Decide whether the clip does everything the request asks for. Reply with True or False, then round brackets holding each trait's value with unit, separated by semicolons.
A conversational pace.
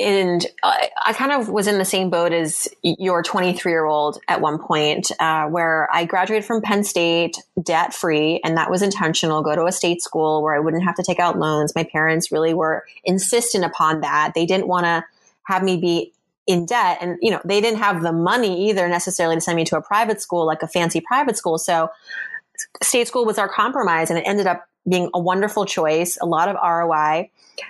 False (215 wpm)